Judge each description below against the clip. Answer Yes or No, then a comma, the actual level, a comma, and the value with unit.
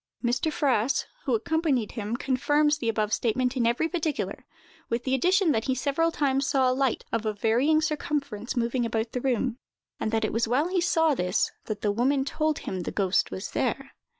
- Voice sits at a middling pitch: No, very high, 255 Hz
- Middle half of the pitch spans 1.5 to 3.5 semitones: No, average, 4.6 semitones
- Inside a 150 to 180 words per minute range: No, average, 200 wpm